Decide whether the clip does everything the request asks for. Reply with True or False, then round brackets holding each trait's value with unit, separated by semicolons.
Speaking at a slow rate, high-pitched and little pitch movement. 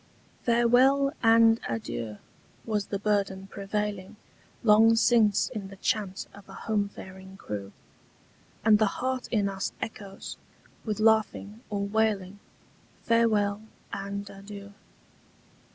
True (115 wpm; 205 Hz; 2.2 semitones)